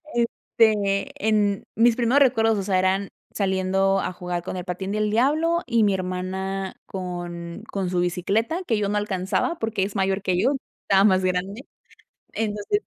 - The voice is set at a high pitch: Yes, high, 195 Hz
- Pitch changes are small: No, average, 3.0 semitones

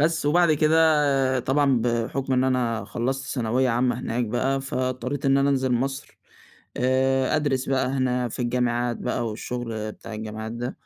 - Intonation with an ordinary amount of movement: No, narrow, 2.2 semitones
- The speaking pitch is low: Yes, low, 130 Hz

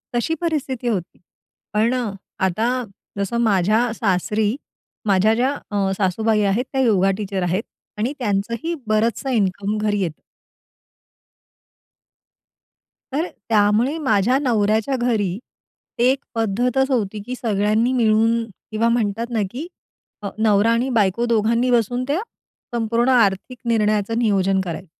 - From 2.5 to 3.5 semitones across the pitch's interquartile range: Yes, average, 3.1 semitones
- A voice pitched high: Yes, high, 220 Hz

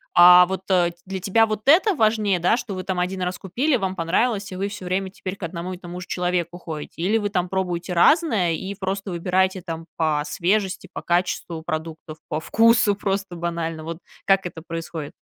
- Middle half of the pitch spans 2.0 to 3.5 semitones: Yes, narrow, 2.5 semitones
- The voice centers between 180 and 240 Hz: Yes, medium, 185 Hz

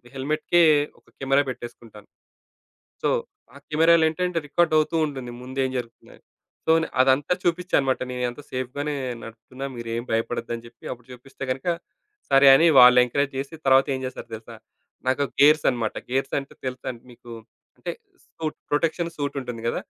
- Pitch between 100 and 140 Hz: Yes, low, 135 Hz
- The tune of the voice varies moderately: Yes, average, 3.2 semitones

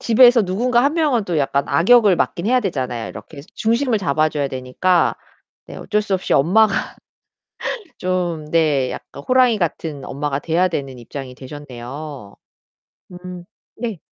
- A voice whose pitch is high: No, medium, 170 Hz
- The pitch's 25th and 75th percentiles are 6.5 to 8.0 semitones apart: Yes, wide, 7.6 semitones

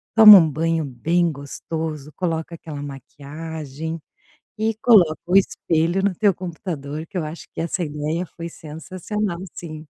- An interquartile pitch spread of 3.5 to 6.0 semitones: No, narrow, 2.6 semitones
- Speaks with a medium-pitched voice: Yes, medium, 165 Hz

